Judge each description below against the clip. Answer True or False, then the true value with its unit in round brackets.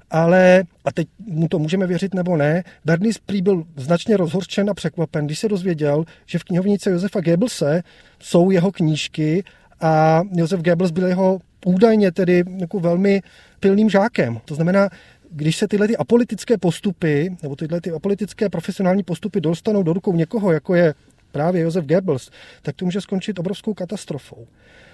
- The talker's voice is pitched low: False (180 Hz)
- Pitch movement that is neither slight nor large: True (3.4 semitones)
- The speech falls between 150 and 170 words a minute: True (160 wpm)